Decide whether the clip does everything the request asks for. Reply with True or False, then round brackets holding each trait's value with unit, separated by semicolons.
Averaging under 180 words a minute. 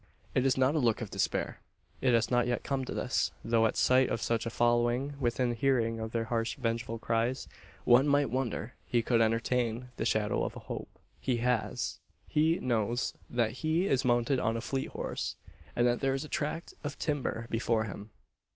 False (195 wpm)